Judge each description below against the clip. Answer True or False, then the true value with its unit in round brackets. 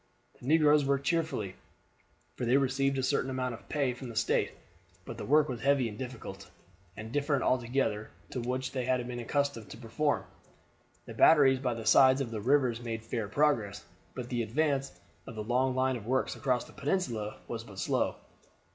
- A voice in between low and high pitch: False (130 Hz)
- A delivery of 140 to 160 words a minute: False (190 wpm)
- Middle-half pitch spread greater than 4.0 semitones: False (3.1 semitones)